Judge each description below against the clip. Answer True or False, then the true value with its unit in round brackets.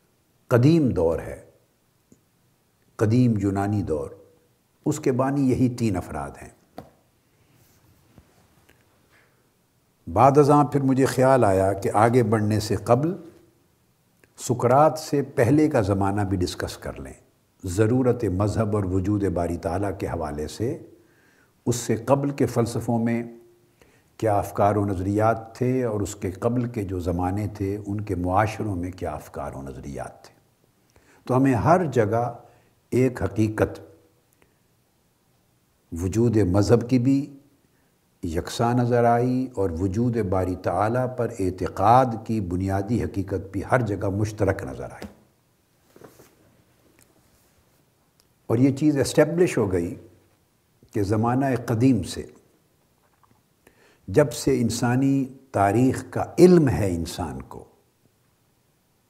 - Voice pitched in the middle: False (115 Hz)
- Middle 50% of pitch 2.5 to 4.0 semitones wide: False (4.6 semitones)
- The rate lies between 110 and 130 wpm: True (120 wpm)